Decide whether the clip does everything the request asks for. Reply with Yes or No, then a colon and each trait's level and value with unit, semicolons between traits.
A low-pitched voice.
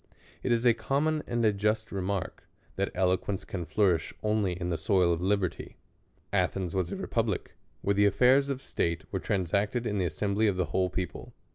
Yes: low, 100 Hz